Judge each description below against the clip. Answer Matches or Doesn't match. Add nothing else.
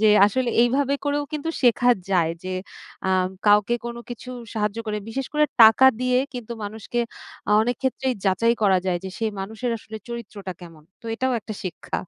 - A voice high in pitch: Matches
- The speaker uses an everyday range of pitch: Matches